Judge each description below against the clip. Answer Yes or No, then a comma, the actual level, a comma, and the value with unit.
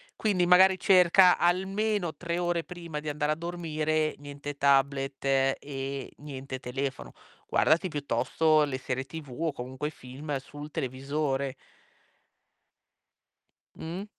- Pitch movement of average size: Yes, average, 4.0 semitones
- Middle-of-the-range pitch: Yes, medium, 150 Hz